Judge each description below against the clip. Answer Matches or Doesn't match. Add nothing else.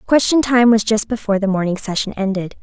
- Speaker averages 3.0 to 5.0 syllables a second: Doesn't match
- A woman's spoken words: Matches